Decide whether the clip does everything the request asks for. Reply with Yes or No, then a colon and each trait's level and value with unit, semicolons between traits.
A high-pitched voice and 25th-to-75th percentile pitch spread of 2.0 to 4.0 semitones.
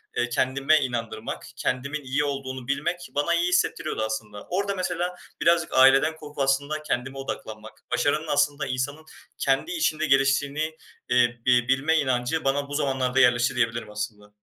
No: low, 135 Hz; average, 3.7 semitones